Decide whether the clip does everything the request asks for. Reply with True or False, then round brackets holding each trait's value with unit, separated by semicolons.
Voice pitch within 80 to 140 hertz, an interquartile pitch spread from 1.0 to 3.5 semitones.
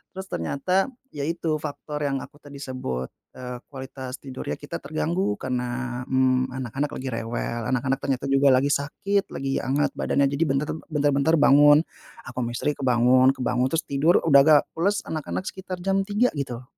True (135 Hz; 2.6 semitones)